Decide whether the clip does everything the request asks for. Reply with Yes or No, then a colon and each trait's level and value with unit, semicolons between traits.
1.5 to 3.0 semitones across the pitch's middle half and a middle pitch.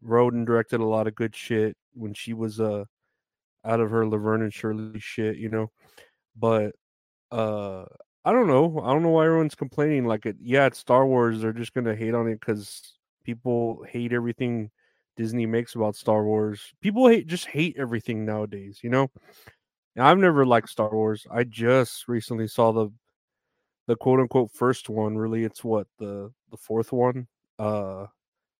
No: narrow, 2.4 semitones; low, 115 Hz